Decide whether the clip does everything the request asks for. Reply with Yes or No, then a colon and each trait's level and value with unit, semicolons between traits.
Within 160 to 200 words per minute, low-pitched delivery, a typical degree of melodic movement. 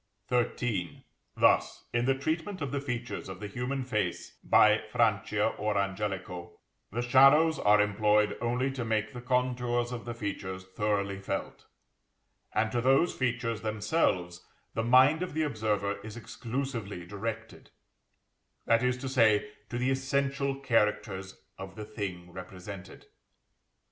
No: average, 140 wpm; low, 115 Hz; average, 4.0 semitones